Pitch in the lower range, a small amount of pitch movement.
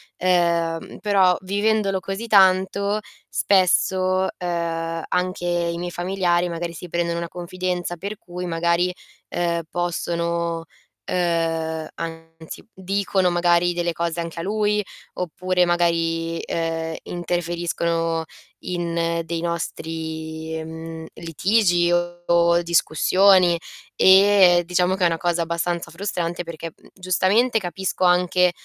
No: medium, 175 Hz; narrow, 1.7 semitones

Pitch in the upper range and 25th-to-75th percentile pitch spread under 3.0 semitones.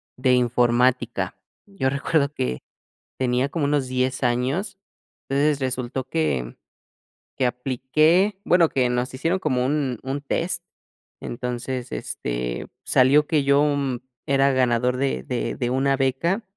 No: low, 130 Hz; narrow, 2.5 semitones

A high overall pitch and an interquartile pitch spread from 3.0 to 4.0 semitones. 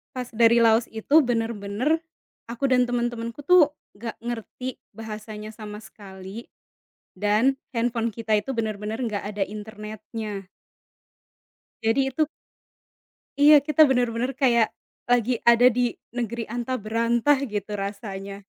No: high, 230 Hz; narrow, 2.6 semitones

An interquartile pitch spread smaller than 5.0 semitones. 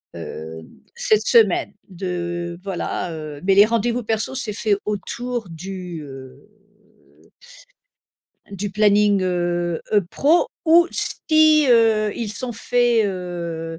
No: average, 5.3 semitones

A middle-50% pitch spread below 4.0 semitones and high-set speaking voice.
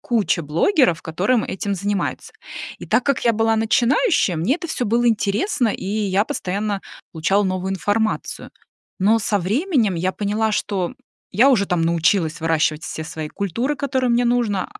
No: average, 4.6 semitones; high, 205 Hz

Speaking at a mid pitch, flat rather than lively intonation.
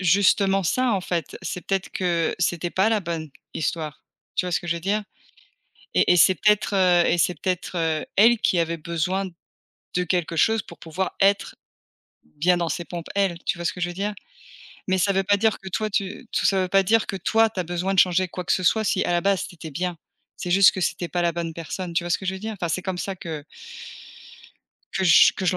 Yes: medium, 180 Hz; narrow, 2.3 semitones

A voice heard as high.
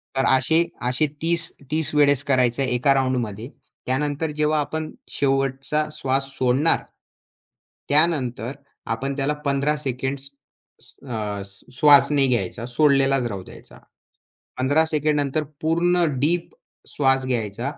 No: low, 135 Hz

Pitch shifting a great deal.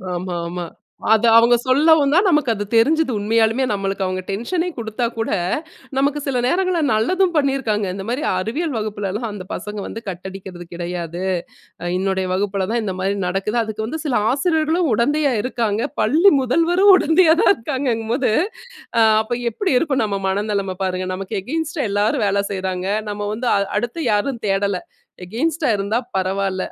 Yes: wide, 6.5 semitones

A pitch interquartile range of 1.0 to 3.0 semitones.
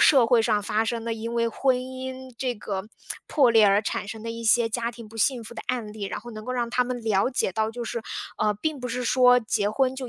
Yes: narrow, 2.4 semitones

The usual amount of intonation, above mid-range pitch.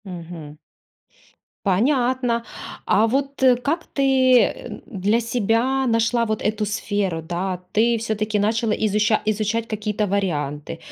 Yes: average, 3.1 semitones; high, 215 Hz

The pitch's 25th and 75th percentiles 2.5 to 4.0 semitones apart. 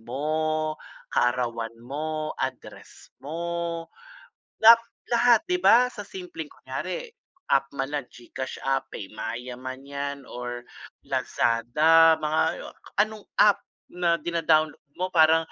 No: average, 4.6 semitones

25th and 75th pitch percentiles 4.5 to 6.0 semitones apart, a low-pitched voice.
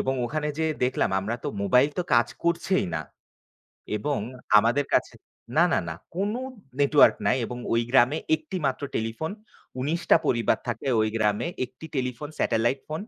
Yes: average, 4.8 semitones; low, 130 Hz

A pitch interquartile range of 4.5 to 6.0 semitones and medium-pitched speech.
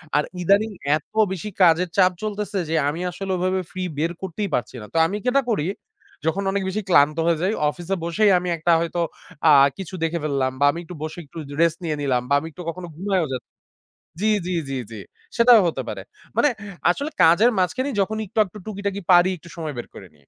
No: average, 3.9 semitones; medium, 180 Hz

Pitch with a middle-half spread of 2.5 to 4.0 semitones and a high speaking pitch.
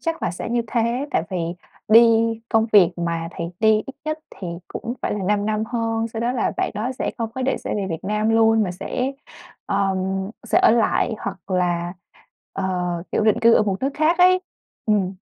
Yes: average, 3.5 semitones; high, 220 Hz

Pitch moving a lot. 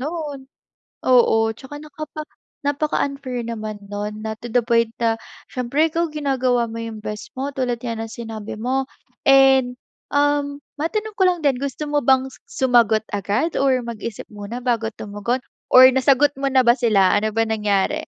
No: average, 4.0 semitones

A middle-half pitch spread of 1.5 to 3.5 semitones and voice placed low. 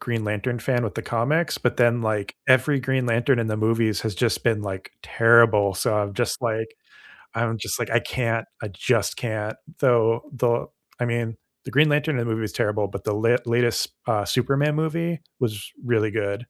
Yes: narrow, 2.4 semitones; low, 115 Hz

